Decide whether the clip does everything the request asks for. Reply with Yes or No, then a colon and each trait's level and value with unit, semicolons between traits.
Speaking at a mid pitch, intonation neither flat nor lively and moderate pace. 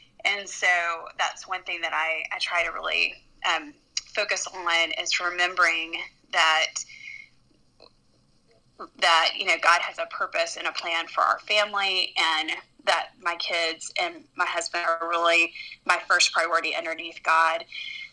Yes: medium, 175 Hz; average, 4.2 semitones; average, 145 wpm